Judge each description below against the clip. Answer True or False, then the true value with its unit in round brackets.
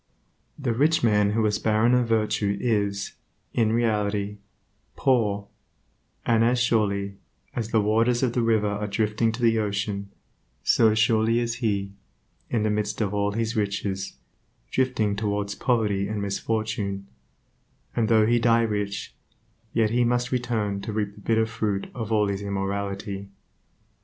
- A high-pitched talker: False (110 Hz)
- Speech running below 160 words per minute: True (150 wpm)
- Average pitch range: False (2.2 semitones)